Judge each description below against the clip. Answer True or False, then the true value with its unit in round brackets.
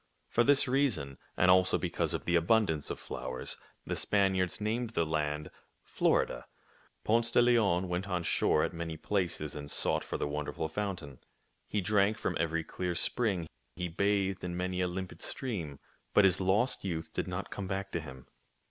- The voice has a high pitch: False (90 Hz)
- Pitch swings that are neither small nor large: True (4.2 semitones)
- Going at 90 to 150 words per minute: False (175 wpm)